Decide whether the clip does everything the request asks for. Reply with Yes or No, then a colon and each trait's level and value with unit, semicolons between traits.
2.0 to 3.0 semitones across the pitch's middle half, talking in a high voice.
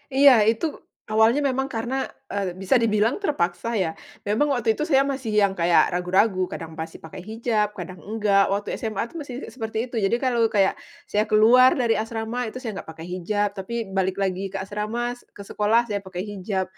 No: average, 3.5 semitones; high, 215 Hz